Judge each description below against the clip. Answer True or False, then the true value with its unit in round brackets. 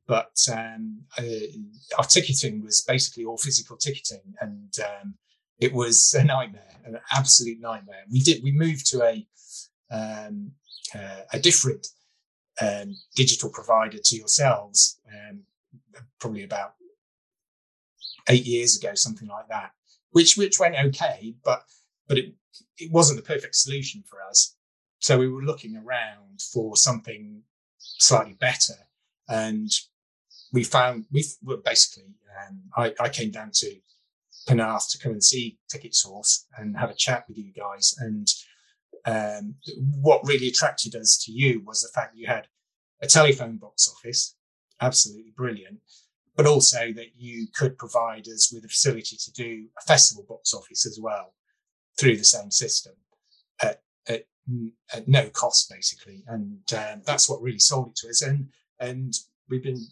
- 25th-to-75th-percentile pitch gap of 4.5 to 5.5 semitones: True (5.1 semitones)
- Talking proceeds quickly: False (155 wpm)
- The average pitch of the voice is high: False (125 Hz)